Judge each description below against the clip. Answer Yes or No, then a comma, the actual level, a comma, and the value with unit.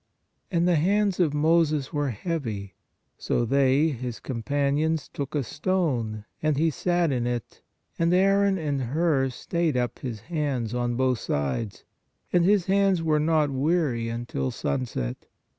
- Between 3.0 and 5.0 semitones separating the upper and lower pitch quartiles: No, wide, 5.6 semitones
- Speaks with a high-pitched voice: No, medium, 145 Hz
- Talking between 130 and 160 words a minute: Yes, average, 145 wpm